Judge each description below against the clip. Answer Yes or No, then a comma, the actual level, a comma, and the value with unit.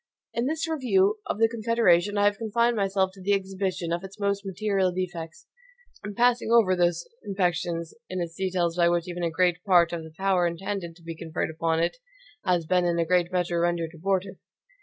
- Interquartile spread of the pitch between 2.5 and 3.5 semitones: Yes, average, 2.8 semitones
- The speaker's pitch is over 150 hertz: Yes, medium, 185 Hz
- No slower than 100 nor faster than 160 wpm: No, average, 195 wpm